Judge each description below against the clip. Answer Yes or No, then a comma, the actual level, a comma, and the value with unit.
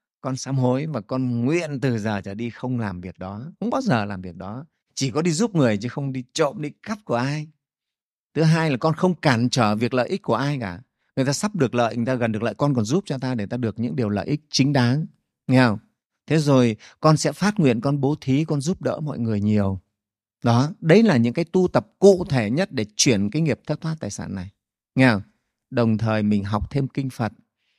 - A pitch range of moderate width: Yes, average, 5.0 semitones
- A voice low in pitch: Yes, low, 130 Hz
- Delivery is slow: No, fast, 250 wpm